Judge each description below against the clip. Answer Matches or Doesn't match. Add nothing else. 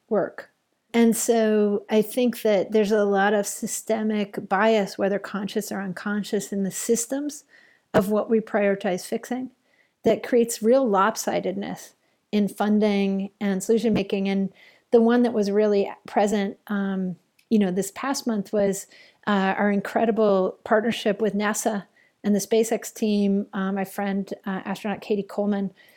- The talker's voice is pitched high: Matches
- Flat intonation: Matches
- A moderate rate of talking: Matches